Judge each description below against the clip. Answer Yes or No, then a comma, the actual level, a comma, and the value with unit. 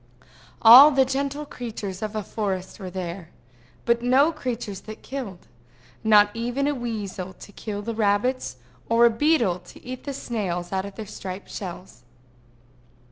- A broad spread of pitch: No, average, 4.6 semitones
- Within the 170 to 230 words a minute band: No, average, 155 wpm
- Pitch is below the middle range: No, high, 220 Hz